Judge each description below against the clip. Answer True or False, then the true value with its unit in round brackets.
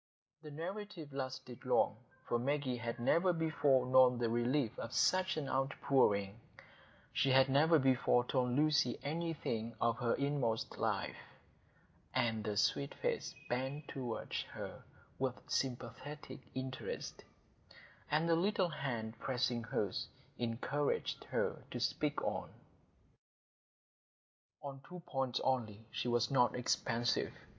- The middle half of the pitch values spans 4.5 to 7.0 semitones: False (3.6 semitones)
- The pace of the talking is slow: True (120 wpm)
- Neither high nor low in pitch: False (130 Hz)